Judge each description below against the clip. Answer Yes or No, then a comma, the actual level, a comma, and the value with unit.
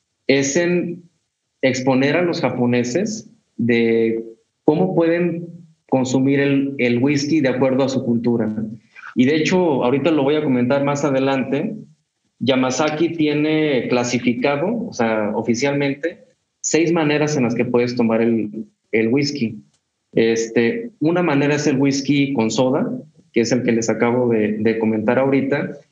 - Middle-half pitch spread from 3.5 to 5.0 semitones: Yes, average, 4.4 semitones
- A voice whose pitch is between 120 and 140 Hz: Yes, low, 135 Hz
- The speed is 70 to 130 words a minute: No, average, 145 wpm